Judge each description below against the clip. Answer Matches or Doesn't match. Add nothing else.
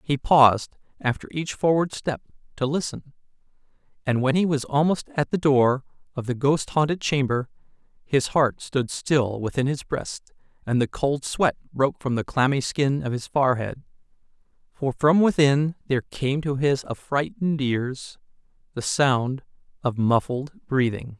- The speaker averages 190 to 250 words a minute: Doesn't match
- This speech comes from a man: Matches